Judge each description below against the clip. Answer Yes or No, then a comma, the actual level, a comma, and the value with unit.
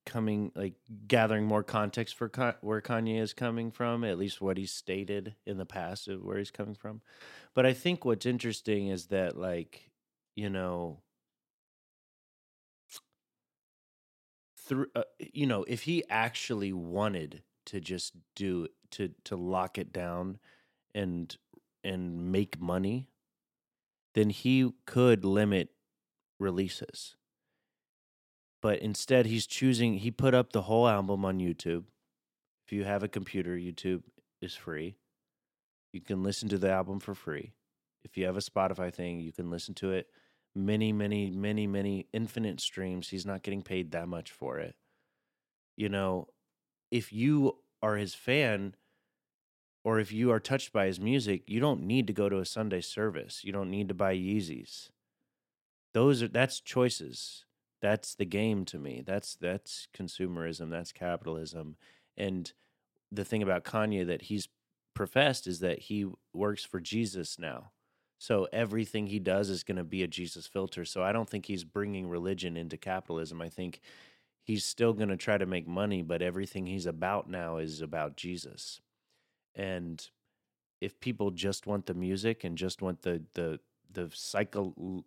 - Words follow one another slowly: No, average, 160 wpm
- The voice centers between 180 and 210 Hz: No, low, 100 Hz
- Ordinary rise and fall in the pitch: Yes, average, 3.1 semitones